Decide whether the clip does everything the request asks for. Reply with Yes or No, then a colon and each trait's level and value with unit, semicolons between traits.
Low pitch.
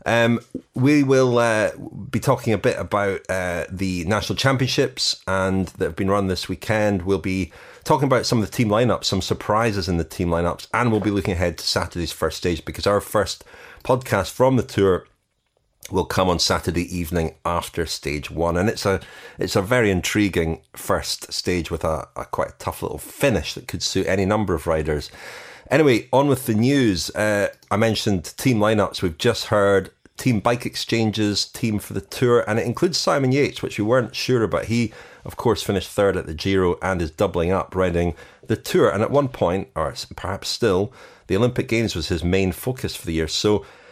Yes: low, 100 Hz